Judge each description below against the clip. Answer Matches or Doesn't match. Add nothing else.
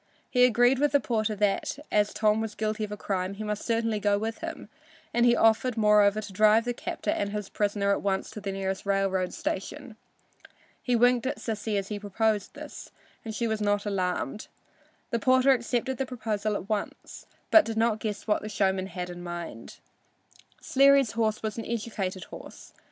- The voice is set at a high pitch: Matches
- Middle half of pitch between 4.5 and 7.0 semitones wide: Doesn't match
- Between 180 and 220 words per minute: Matches